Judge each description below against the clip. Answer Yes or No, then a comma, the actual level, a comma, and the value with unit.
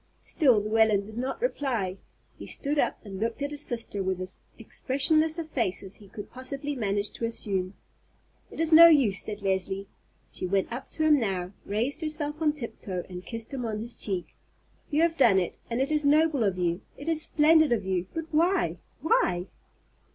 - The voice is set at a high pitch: Yes, high, 235 Hz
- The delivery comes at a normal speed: Yes, average, 190 wpm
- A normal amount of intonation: No, wide, 7.3 semitones